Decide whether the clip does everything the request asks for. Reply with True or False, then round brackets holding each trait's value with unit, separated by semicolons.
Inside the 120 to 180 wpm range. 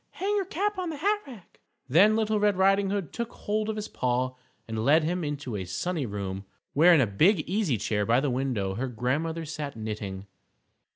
False (205 wpm)